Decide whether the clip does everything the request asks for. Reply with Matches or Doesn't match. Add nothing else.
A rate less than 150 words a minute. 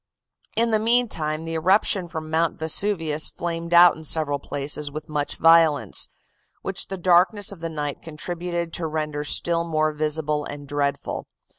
Doesn't match